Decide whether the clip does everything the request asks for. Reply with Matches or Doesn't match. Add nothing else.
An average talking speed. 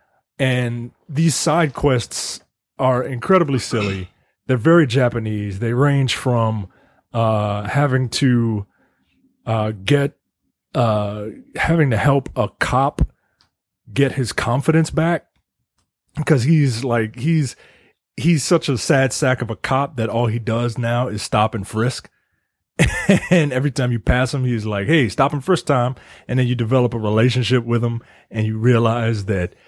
Matches